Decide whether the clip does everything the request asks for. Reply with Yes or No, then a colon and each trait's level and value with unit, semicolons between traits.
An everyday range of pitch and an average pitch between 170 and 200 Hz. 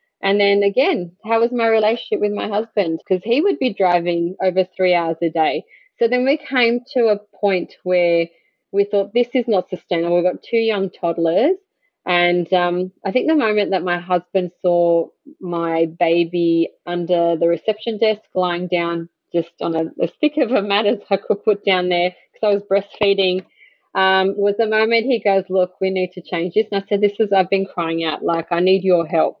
Yes: average, 3.7 semitones; high, 190 Hz